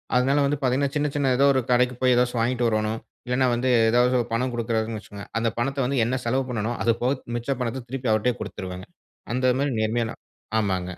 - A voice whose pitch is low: Yes, low, 125 Hz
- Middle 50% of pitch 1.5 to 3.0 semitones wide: Yes, narrow, 2.4 semitones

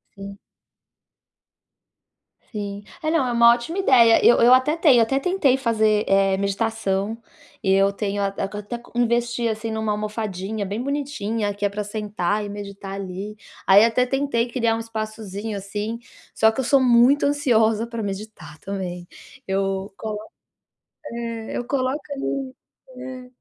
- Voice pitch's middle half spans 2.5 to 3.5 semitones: Yes, average, 3.2 semitones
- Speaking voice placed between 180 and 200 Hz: No, high, 220 Hz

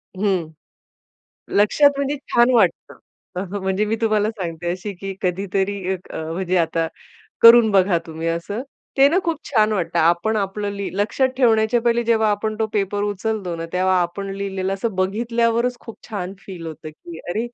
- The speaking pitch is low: No, high, 200 Hz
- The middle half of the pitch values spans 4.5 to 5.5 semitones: No, average, 3.5 semitones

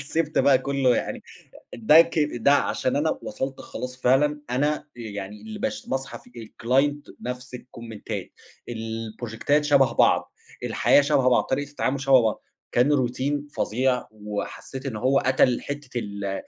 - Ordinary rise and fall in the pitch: Yes, average, 3.2 semitones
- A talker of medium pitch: No, low, 130 Hz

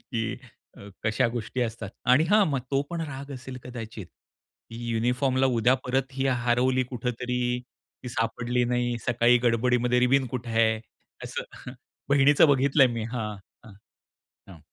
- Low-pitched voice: Yes, low, 125 Hz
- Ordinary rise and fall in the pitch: No, narrow, 2.1 semitones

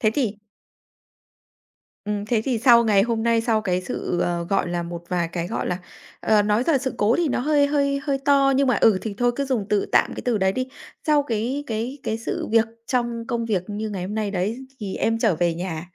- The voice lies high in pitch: Yes, high, 220 Hz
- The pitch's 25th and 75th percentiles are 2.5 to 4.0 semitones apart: No, average, 4.4 semitones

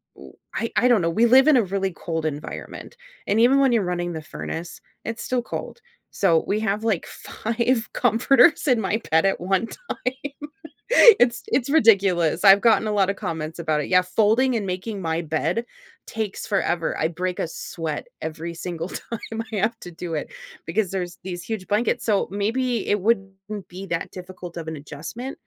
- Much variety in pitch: No, average, 5.0 semitones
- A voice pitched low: No, high, 195 Hz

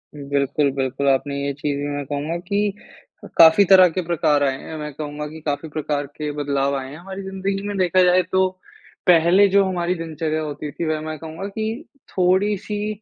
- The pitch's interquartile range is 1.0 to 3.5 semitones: No, average, 4.6 semitones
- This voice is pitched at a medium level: Yes, medium, 160 Hz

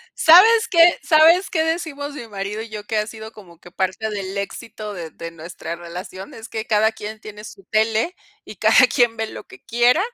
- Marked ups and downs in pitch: Yes, wide, 6.3 semitones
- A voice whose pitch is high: Yes, high, 220 Hz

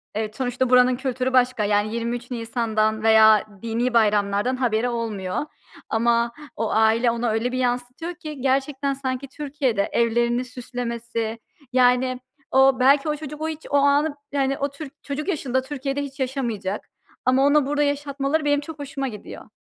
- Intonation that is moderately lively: Yes, average, 3.1 semitones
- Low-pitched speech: No, very high, 255 Hz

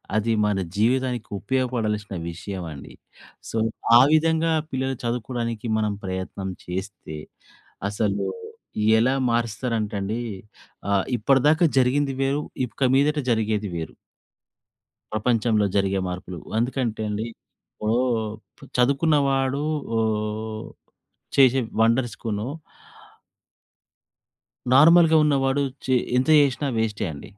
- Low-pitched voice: Yes, low, 115 Hz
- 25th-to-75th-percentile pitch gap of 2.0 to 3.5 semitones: No, average, 4.1 semitones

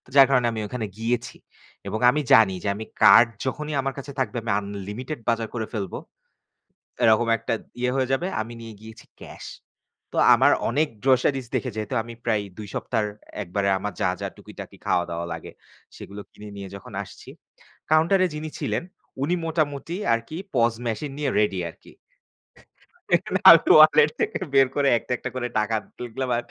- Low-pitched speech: Yes, low, 120 Hz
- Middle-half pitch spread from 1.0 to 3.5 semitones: No, average, 4.1 semitones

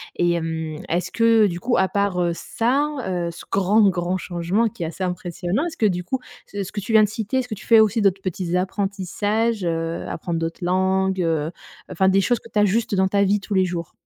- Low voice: No, high, 190 Hz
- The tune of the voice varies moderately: Yes, average, 3.3 semitones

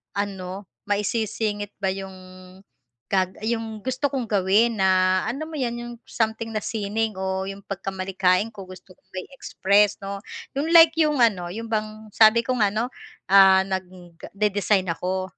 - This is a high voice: Yes, high, 205 Hz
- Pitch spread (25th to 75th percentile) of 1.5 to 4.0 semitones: Yes, average, 2.9 semitones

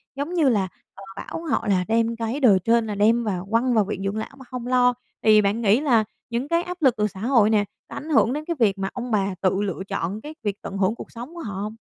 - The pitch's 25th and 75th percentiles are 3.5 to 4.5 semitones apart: Yes, average, 3.9 semitones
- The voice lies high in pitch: Yes, high, 225 Hz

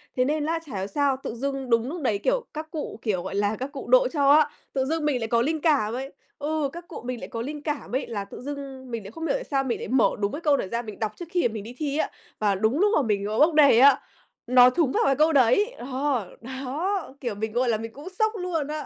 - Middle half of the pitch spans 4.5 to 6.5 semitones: Yes, average, 4.8 semitones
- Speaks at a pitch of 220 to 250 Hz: No, very high, 270 Hz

